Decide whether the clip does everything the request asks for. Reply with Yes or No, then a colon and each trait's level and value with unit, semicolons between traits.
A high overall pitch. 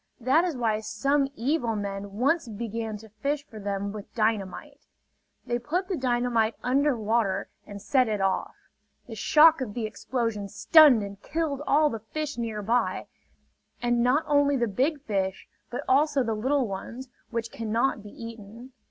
Yes: high, 235 Hz